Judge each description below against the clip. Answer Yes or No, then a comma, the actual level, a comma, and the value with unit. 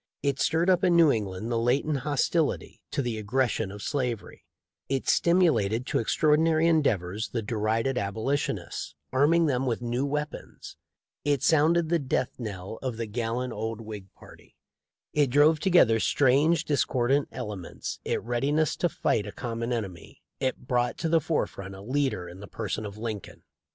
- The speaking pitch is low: Yes, low, 125 Hz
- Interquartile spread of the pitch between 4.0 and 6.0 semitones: Yes, average, 5.1 semitones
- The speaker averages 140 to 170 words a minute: Yes, average, 160 wpm